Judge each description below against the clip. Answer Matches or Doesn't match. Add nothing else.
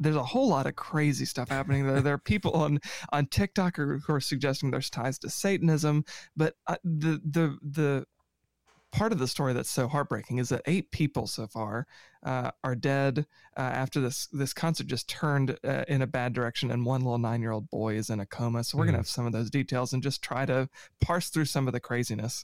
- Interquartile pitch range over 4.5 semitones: Doesn't match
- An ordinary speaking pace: Doesn't match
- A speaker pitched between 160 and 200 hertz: Doesn't match